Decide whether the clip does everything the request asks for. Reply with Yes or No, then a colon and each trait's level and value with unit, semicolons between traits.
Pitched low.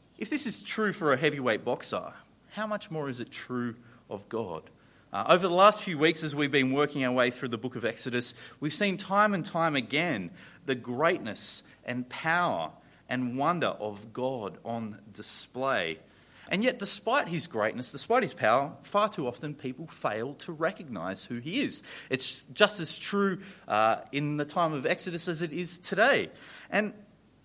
No: medium, 145 Hz